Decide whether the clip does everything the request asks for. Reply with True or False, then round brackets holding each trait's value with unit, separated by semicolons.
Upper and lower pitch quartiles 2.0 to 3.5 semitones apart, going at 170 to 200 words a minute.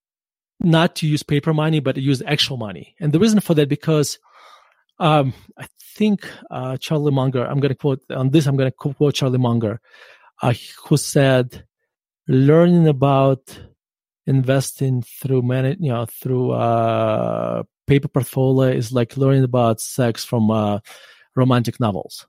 False (3.2 semitones; 155 wpm)